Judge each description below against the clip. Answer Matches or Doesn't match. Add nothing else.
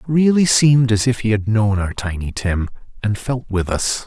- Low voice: Matches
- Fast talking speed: Matches